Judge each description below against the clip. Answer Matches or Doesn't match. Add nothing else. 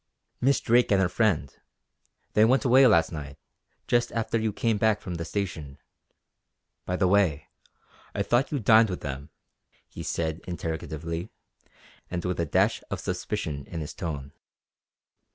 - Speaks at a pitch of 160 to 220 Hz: Doesn't match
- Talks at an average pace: Matches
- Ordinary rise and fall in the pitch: Doesn't match